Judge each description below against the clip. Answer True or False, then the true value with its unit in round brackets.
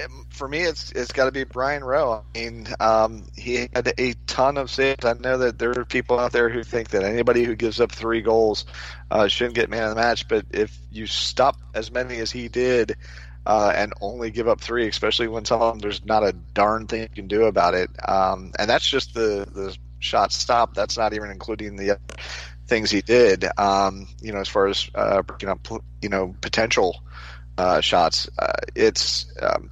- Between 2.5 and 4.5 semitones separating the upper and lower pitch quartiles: True (4.1 semitones)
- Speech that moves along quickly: True (215 wpm)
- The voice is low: True (110 Hz)